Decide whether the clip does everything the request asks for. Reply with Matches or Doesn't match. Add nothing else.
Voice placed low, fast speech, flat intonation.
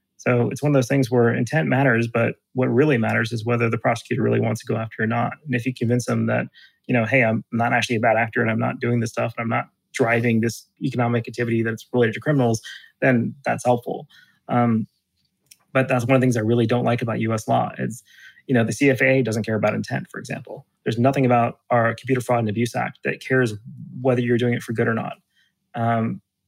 Matches